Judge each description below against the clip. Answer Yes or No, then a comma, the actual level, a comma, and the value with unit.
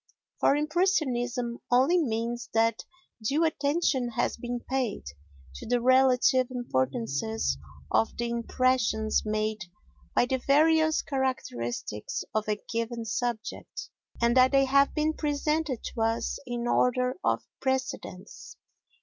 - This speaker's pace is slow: Yes, slow, 120 wpm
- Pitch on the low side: No, high, 245 Hz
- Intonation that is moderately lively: Yes, average, 3.3 semitones